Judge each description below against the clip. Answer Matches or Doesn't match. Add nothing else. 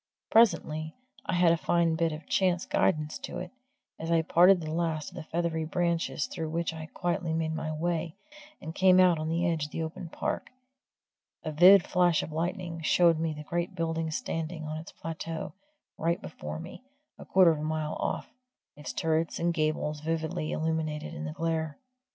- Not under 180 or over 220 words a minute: Matches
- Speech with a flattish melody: Matches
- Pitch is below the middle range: Doesn't match